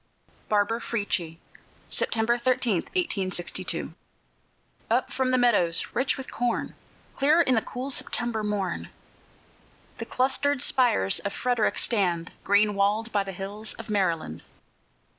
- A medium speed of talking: No, slow, 125 wpm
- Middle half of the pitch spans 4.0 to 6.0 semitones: Yes, average, 4.3 semitones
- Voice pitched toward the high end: Yes, high, 220 Hz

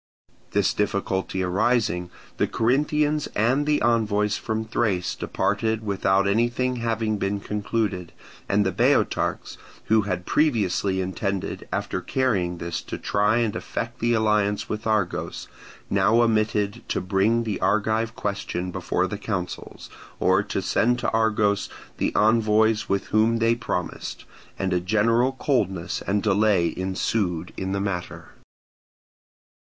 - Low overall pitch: Yes, low, 105 Hz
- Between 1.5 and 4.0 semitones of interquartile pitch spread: Yes, average, 2.9 semitones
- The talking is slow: Yes, slow, 130 wpm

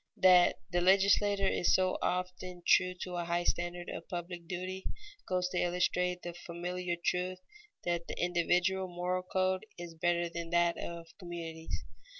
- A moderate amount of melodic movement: No, narrow, 1.0 semitones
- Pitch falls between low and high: Yes, medium, 180 Hz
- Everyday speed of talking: Yes, average, 155 wpm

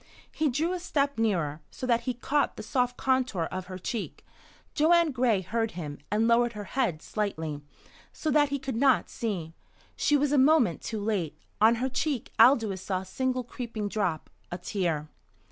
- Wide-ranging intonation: Yes, wide, 5.9 semitones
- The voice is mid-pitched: No, high, 230 Hz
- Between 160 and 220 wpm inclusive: Yes, average, 180 wpm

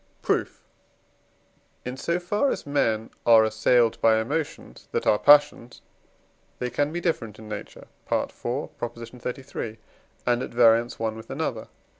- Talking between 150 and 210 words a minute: No, slow, 135 wpm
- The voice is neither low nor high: No, low, 120 Hz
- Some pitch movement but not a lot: Yes, average, 4.1 semitones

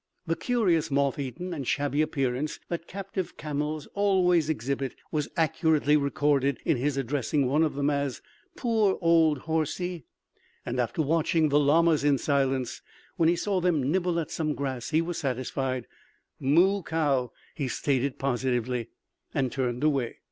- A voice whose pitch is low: No, medium, 150 Hz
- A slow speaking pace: No, average, 150 wpm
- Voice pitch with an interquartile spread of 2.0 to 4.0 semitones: Yes, average, 3.5 semitones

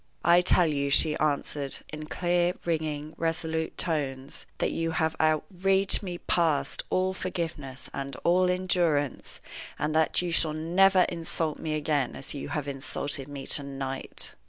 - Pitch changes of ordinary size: Yes, average, 3.3 semitones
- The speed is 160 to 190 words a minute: No, average, 150 wpm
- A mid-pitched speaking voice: Yes, medium, 160 Hz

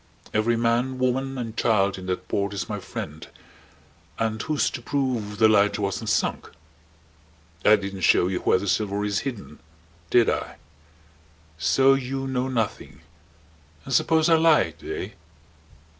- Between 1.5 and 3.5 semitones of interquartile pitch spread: No, average, 4.7 semitones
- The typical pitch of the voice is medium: No, low, 110 Hz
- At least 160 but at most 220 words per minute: No, average, 145 wpm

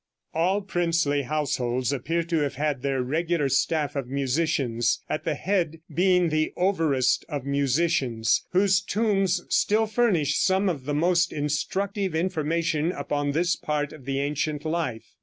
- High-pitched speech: No, medium, 155 Hz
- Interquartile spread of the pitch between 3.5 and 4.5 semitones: Yes, average, 3.9 semitones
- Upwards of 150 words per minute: No, average, 145 wpm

